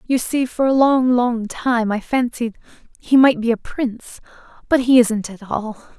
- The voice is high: Yes, high, 240 Hz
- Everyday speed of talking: Yes, average, 190 wpm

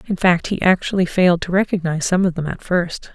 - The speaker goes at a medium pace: No, fast, 230 wpm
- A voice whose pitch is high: No, medium, 180 Hz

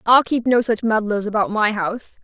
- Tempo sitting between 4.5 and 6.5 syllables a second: Yes, 5.3 syllables/s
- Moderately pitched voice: No, high, 220 Hz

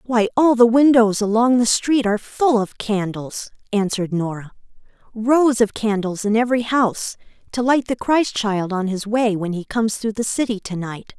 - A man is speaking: No, female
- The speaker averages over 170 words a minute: Yes, average, 190 wpm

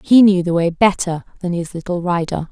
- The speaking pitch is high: No, medium, 175 Hz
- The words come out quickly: Yes, fast, 215 wpm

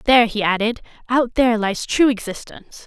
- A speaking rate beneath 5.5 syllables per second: No, 5.7 syllables/s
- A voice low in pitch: No, high, 230 Hz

